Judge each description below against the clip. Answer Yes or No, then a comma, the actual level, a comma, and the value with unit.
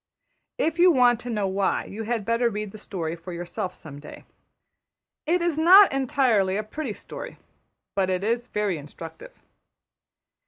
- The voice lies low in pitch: No, high, 215 Hz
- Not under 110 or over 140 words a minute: No, average, 160 wpm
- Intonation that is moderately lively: No, wide, 5.7 semitones